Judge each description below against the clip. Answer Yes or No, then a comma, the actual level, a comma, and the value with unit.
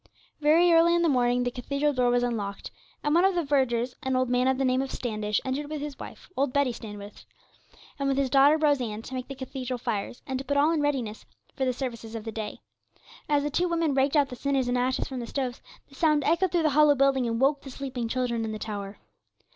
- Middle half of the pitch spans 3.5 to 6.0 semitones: No, average, 3.1 semitones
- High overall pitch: Yes, very high, 265 Hz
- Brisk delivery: Yes, fast, 245 wpm